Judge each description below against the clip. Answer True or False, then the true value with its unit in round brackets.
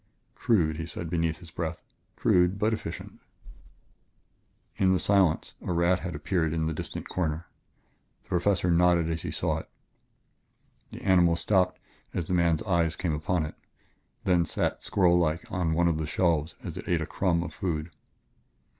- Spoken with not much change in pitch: True (2.1 semitones)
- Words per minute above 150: True (165 wpm)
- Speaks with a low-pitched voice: True (85 Hz)